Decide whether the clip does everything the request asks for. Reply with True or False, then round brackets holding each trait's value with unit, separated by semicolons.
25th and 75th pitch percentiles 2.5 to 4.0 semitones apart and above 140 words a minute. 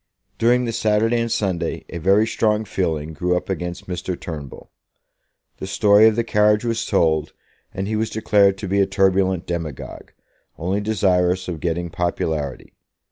True (3.5 semitones; 160 wpm)